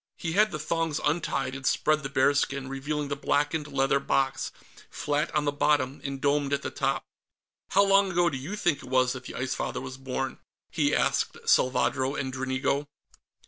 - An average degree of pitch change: No, narrow, 2.3 semitones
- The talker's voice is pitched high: No, medium, 140 Hz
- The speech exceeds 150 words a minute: Yes, average, 185 wpm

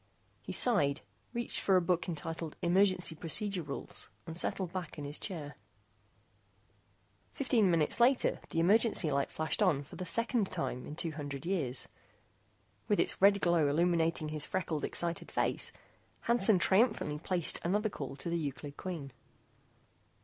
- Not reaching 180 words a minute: Yes, average, 150 wpm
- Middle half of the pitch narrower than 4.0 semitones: No, average, 4.3 semitones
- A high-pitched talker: No, medium, 170 Hz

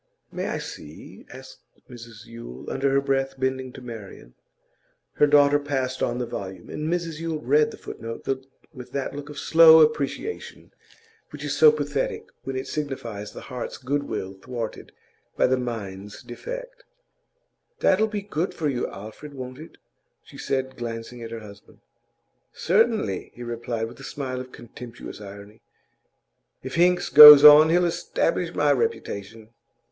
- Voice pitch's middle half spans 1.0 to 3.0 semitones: No, average, 4.8 semitones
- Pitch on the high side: No, low, 130 Hz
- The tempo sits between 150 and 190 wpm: Yes, average, 155 wpm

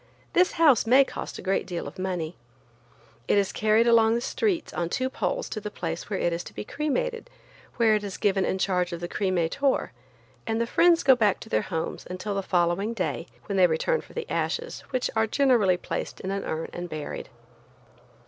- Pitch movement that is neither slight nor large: No, wide, 6.0 semitones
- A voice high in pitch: Yes, high, 205 Hz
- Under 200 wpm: No, fast, 205 wpm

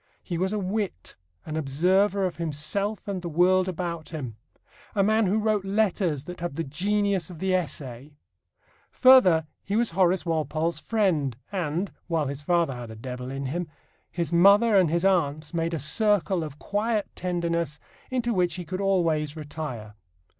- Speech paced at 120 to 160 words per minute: No, average, 170 wpm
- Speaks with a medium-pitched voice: Yes, medium, 175 Hz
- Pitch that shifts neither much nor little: Yes, average, 4.3 semitones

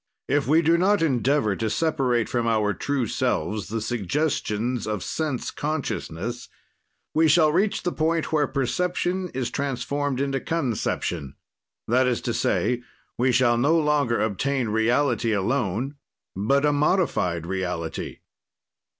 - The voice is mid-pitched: No, low, 130 Hz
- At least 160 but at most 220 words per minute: No, slow, 135 wpm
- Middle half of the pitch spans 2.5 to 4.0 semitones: No, average, 5.1 semitones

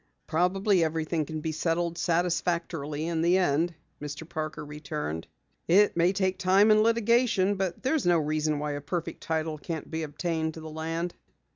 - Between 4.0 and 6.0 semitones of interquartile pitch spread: No, average, 3.0 semitones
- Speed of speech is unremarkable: Yes, average, 165 wpm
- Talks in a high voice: No, medium, 165 Hz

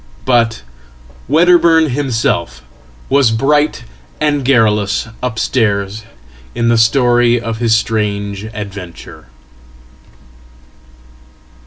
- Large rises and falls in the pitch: No, average, 4.0 semitones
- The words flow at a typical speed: No, slow, 65 wpm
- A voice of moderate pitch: No, low, 115 Hz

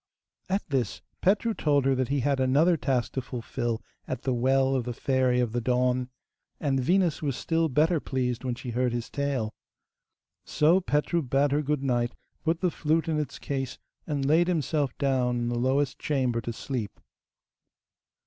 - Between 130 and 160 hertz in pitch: Yes, low, 135 Hz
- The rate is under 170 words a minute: No, average, 175 wpm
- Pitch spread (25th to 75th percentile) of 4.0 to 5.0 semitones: No, average, 3.3 semitones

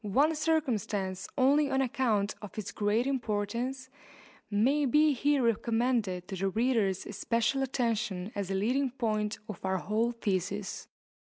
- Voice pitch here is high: Yes, high, 225 Hz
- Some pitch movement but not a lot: Yes, average, 4.4 semitones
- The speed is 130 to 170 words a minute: Yes, average, 140 wpm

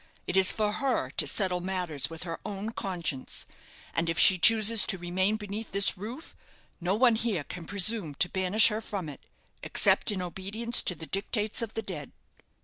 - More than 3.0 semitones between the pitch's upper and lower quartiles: Yes, average, 3.5 semitones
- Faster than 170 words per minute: Yes, average, 185 wpm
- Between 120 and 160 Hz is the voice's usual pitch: No, high, 190 Hz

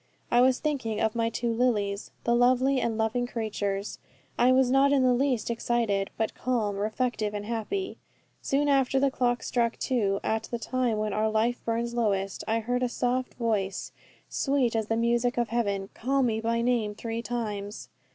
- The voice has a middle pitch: No, high, 235 Hz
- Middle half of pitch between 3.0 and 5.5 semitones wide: No, narrow, 2.5 semitones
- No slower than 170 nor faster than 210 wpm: Yes, average, 180 wpm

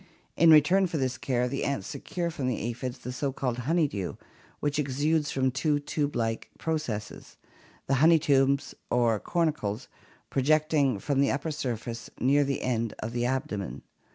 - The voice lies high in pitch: No, low, 135 Hz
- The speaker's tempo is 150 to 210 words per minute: Yes, average, 165 wpm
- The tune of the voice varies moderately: Yes, average, 3.8 semitones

